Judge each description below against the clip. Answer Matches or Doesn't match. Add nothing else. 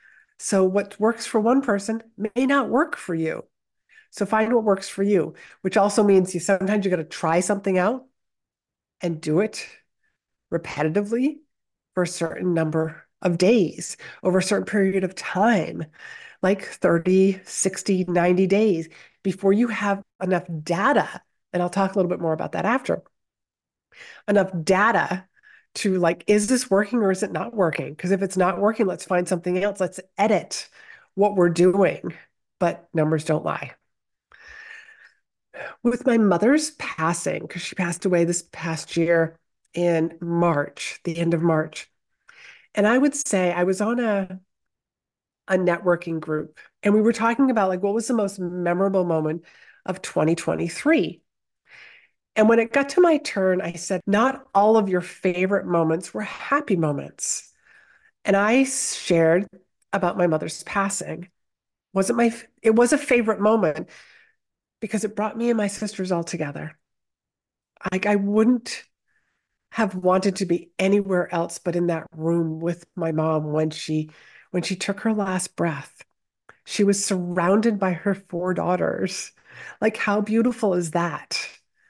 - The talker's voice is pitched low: Doesn't match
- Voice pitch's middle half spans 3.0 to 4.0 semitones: Matches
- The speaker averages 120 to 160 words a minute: Matches